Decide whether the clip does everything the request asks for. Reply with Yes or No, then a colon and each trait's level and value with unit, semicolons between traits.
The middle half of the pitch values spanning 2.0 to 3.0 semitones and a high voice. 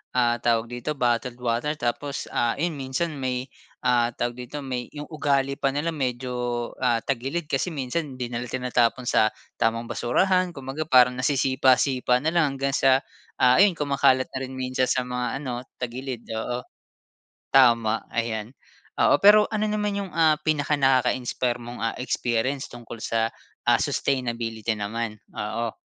No: average, 2.7 semitones; low, 130 Hz